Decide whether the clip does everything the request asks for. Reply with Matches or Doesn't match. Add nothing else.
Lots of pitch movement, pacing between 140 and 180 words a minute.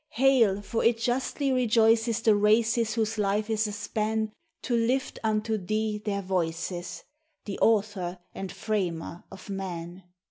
Doesn't match